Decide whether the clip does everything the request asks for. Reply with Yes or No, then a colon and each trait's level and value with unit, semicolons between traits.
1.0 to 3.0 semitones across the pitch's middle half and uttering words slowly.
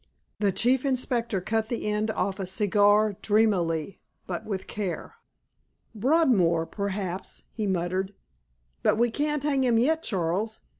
No: average, 3.8 semitones; slow, 130 wpm